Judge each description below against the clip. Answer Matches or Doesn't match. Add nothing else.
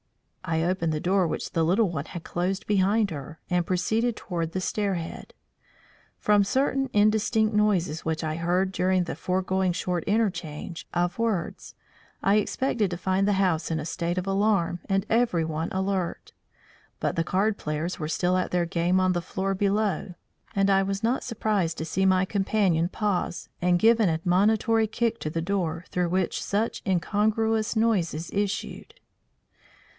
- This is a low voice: Doesn't match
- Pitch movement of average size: Matches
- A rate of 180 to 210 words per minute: Doesn't match